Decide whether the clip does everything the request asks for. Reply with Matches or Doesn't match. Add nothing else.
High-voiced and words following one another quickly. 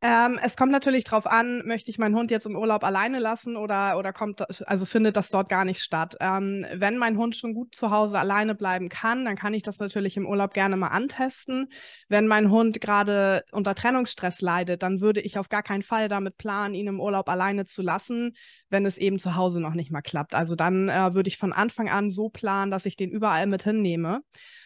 Matches